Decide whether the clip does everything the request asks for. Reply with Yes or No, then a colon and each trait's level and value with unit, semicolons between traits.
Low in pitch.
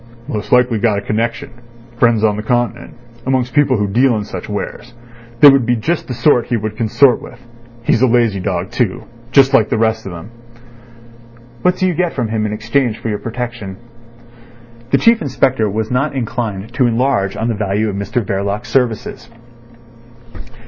Yes: low, 115 Hz